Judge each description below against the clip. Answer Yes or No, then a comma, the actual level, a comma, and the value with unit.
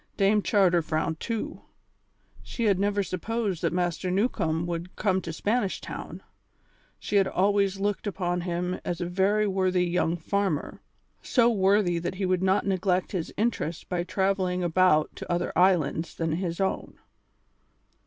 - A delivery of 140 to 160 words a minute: Yes, average, 155 wpm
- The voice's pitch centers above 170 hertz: Yes, medium, 185 Hz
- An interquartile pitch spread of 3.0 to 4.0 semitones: No, narrow, 2.4 semitones